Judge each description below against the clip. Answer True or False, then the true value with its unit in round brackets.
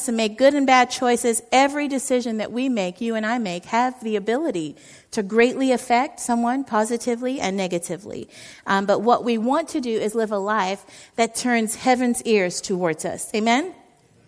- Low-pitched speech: False (235 Hz)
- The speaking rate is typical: True (180 wpm)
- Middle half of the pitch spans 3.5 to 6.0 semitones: False (3.1 semitones)